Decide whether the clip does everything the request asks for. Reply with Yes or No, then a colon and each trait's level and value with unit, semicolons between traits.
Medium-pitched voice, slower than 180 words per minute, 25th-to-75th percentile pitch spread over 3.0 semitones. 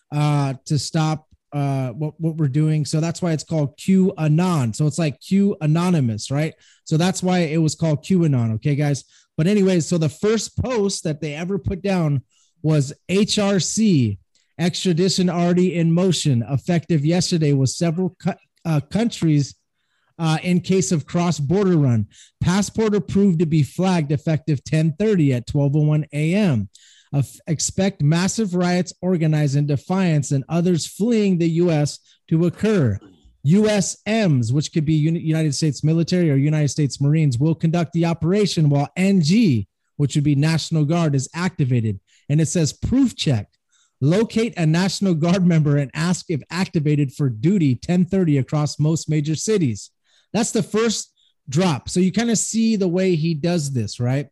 Yes: medium, 160 Hz; average, 160 wpm; average, 3.9 semitones